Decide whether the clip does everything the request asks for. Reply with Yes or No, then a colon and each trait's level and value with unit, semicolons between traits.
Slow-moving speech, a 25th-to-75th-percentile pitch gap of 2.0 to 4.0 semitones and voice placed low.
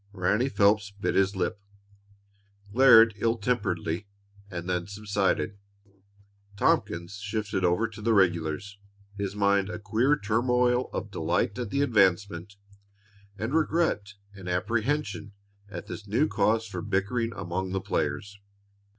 Yes: slow, 125 wpm; average, 3.0 semitones; low, 100 Hz